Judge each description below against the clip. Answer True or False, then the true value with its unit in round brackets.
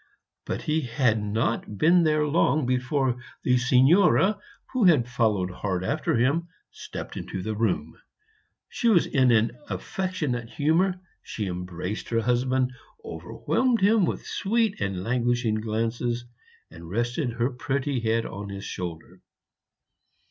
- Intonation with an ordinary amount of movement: False (5.9 semitones)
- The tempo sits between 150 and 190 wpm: False (135 wpm)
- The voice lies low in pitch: True (125 Hz)